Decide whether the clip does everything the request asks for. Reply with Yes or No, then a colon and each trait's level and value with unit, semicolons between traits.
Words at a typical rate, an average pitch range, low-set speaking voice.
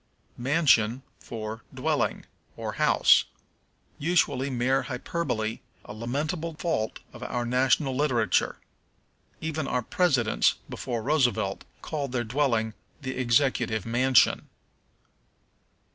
No: slow, 100 wpm; average, 4.0 semitones; low, 130 Hz